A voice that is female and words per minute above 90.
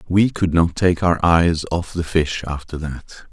No: male; average, 200 wpm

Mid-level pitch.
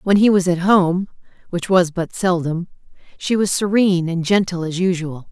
Yes: medium, 180 Hz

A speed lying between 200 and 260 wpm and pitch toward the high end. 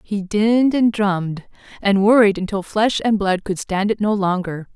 No: average, 190 wpm; high, 200 Hz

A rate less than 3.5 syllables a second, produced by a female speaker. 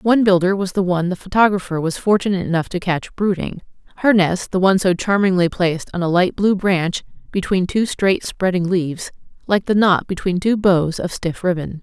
No: 5.5 syllables/s; female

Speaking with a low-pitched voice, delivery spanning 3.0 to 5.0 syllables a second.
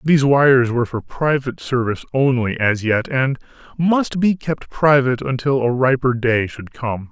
Yes: low, 130 Hz; 4.9 syllables/s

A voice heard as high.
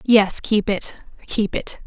Yes: high, 205 Hz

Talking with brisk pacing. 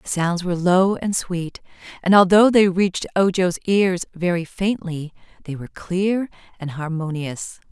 No: average, 150 wpm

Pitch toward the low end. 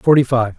Yes: low, 125 Hz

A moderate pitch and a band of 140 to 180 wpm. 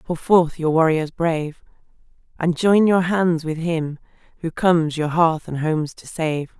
Yes: medium, 165 Hz; average, 175 wpm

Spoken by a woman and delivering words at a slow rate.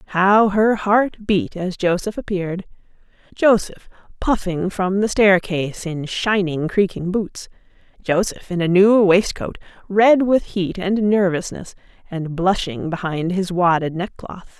Yes: female; slow, 125 wpm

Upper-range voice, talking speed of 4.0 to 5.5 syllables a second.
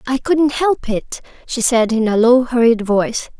Yes: high, 245 Hz; 4.4 syllables/s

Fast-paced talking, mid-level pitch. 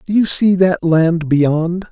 No: average, 190 wpm; medium, 170 Hz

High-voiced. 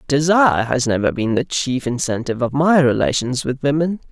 No: low, 135 Hz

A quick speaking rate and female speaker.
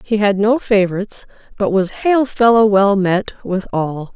No: average, 175 wpm; female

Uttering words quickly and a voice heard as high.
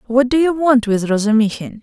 No: average, 195 wpm; high, 240 Hz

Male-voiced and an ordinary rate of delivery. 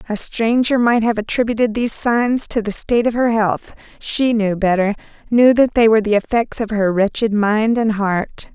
No: female; average, 195 wpm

